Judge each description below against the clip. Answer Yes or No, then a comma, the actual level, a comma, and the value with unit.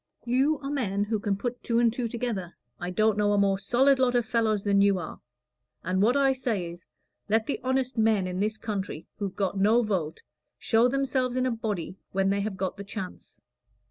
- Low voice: No, high, 215 Hz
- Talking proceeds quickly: Yes, fast, 210 wpm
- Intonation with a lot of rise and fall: No, average, 3.9 semitones